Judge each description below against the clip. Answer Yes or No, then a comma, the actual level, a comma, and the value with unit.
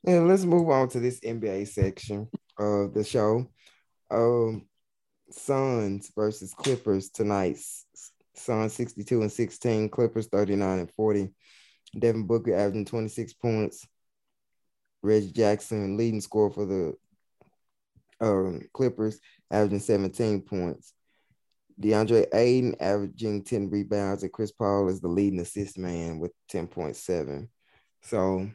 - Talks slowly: Yes, slow, 120 wpm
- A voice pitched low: Yes, low, 105 Hz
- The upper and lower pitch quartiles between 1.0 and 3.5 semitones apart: Yes, narrow, 2.5 semitones